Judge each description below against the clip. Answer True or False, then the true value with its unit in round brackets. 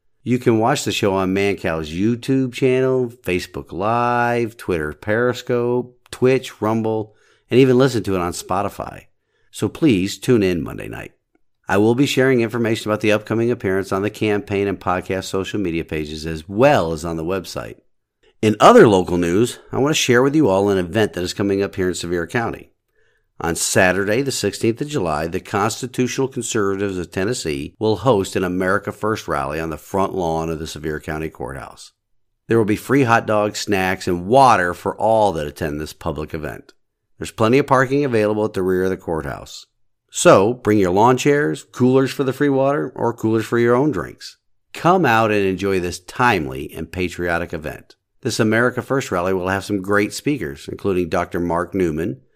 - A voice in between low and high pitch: False (105 Hz)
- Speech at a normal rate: True (185 wpm)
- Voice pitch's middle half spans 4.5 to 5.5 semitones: True (4.9 semitones)